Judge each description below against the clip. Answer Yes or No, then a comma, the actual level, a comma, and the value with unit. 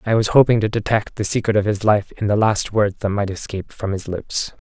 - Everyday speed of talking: No, fast, 255 wpm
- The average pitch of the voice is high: No, low, 105 Hz